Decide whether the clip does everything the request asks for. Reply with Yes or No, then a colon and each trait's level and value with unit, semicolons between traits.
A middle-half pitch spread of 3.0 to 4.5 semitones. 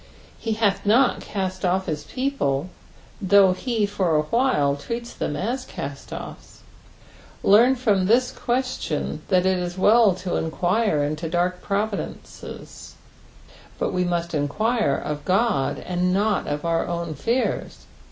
No: average, 5.1 semitones